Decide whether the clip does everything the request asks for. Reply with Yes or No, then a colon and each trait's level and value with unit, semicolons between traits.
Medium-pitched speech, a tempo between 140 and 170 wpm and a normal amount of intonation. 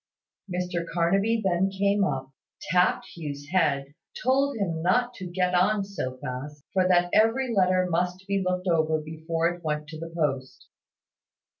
Yes: medium, 180 Hz; average, 155 wpm; average, 3.6 semitones